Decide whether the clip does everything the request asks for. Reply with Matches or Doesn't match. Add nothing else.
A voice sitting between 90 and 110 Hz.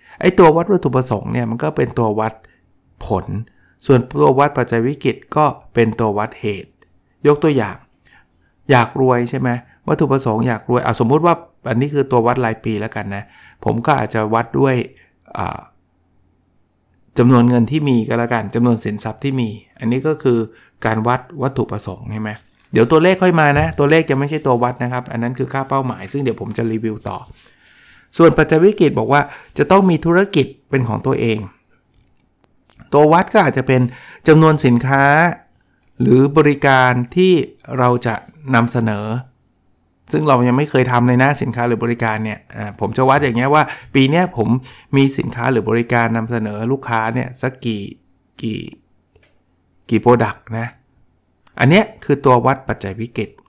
Doesn't match